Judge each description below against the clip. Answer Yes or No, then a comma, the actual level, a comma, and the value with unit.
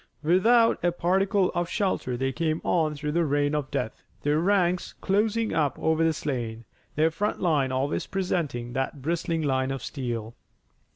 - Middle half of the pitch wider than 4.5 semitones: Yes, average, 5.0 semitones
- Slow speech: No, average, 165 wpm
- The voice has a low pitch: No, medium, 155 Hz